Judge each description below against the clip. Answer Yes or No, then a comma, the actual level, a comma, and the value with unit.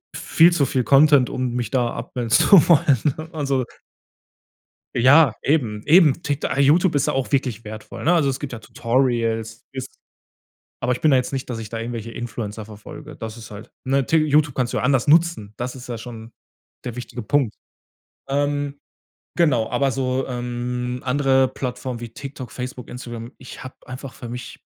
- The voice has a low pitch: Yes, low, 130 Hz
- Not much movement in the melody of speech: No, average, 3.0 semitones